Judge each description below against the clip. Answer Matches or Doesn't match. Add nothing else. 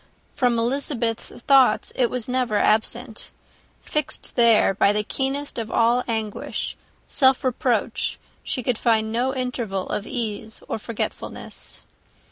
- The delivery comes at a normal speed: Doesn't match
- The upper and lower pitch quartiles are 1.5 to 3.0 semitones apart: Matches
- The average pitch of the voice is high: Matches